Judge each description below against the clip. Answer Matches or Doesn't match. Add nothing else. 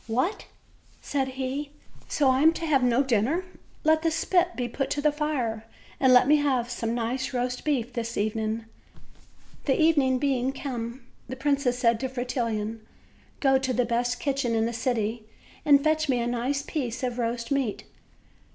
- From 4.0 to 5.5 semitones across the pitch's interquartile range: Doesn't match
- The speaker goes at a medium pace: Matches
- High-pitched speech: Matches